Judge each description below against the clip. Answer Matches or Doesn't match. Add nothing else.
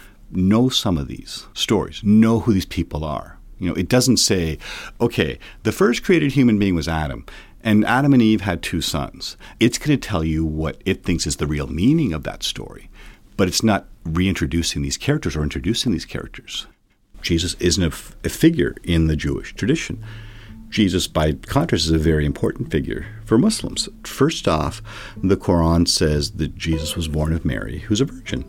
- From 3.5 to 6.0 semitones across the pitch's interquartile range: Matches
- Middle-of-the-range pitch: Doesn't match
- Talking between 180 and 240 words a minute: Matches